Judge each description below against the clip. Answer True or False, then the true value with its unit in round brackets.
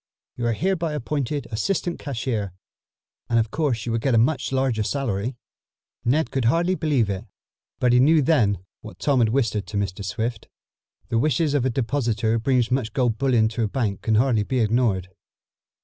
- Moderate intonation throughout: True (3.9 semitones)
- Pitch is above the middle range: False (120 Hz)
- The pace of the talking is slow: False (185 wpm)